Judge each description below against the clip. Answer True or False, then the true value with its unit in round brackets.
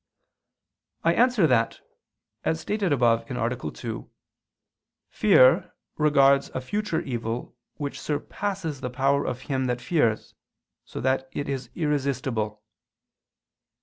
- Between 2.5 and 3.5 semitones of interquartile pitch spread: False (4.1 semitones)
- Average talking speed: False (115 wpm)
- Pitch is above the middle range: False (135 Hz)